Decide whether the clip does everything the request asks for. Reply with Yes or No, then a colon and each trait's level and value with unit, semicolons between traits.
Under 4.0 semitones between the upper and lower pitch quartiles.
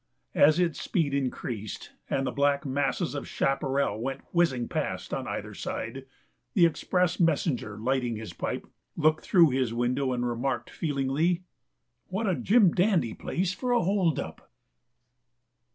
No: average, 5.2 semitones